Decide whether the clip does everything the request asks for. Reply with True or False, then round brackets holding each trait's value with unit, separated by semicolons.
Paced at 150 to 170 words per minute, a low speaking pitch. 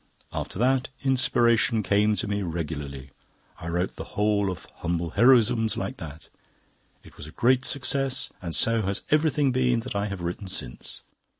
True (165 wpm; 105 Hz)